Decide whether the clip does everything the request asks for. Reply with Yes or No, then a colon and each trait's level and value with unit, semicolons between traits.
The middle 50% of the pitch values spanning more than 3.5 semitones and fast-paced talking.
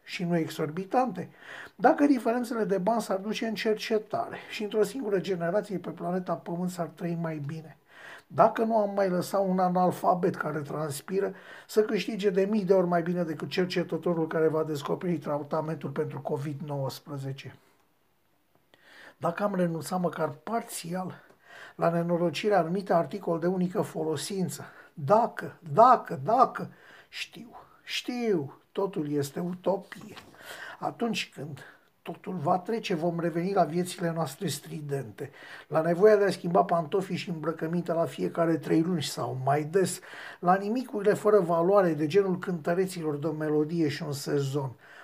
No: average, 3.9 semitones; average, 140 wpm